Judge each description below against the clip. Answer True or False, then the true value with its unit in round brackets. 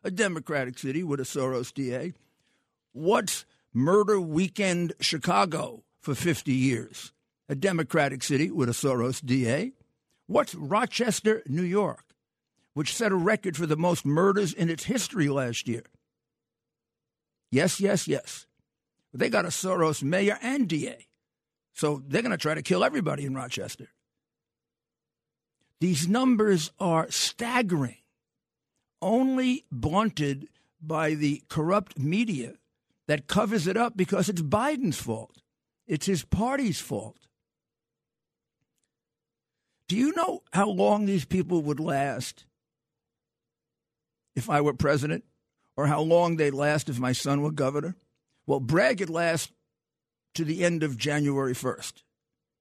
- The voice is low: False (160 Hz)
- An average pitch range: False (5.8 semitones)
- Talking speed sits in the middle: False (130 wpm)